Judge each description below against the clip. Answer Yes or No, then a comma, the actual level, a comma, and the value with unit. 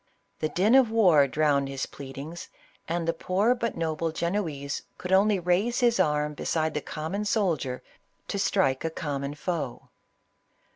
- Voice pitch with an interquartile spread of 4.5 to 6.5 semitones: Yes, average, 5.1 semitones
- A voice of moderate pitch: Yes, medium, 165 Hz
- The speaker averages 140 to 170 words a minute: Yes, average, 155 wpm